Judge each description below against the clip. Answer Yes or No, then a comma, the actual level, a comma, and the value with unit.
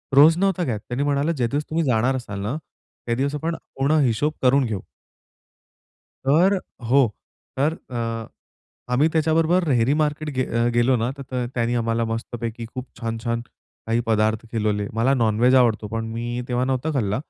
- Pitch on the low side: Yes, low, 125 Hz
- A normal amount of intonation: Yes, average, 3.8 semitones